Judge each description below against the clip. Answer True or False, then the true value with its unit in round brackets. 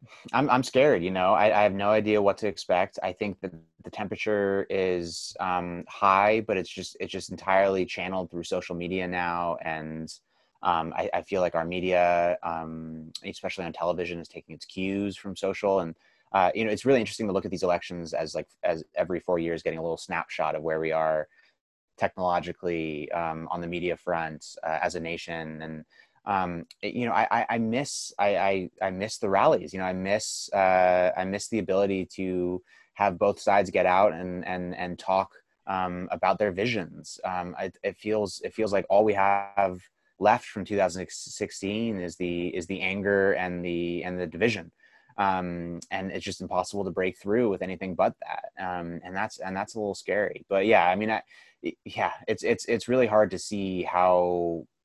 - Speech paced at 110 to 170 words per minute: False (200 wpm)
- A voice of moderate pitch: False (90 Hz)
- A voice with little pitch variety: True (2.1 semitones)